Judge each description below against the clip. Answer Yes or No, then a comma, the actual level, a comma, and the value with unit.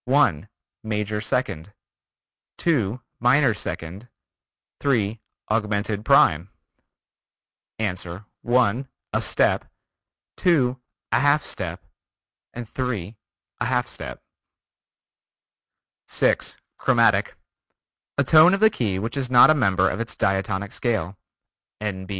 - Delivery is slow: Yes, slow, 105 wpm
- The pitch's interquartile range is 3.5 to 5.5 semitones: Yes, average, 4.4 semitones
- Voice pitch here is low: Yes, low, 110 Hz